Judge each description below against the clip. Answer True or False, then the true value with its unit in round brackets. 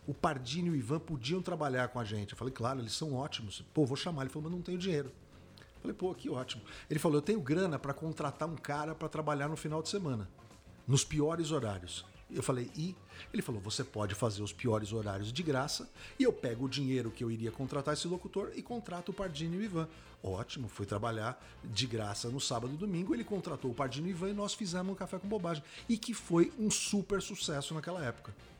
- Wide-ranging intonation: True (6.8 semitones)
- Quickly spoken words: True (230 wpm)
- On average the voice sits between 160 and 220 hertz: False (145 Hz)